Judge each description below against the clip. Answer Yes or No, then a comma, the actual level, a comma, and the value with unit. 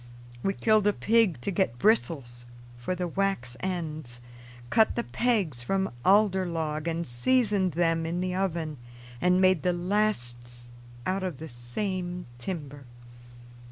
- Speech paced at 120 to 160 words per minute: Yes, average, 140 wpm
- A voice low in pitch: No, medium, 175 Hz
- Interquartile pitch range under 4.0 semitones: No, average, 5.1 semitones